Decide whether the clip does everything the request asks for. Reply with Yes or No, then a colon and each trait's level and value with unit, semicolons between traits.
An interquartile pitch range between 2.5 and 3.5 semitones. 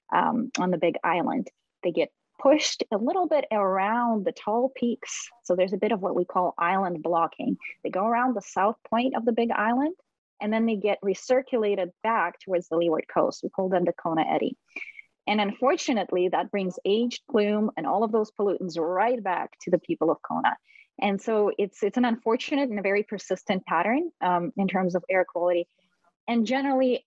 No: average, 5.1 semitones